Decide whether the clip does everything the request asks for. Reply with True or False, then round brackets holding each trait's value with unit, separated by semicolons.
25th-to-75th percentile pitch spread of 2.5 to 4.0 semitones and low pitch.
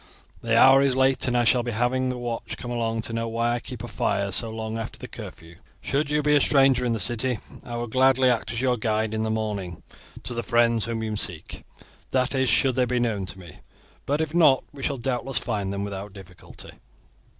True (2.9 semitones; 120 Hz)